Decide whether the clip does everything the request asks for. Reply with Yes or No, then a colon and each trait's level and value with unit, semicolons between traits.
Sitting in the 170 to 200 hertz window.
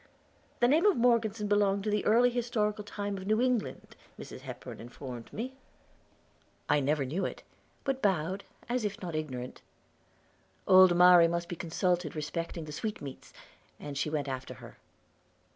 Yes: high, 190 Hz